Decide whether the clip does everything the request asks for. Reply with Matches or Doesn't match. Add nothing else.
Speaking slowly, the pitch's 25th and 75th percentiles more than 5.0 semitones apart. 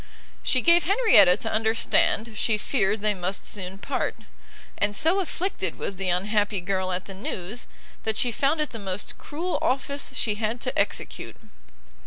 Doesn't match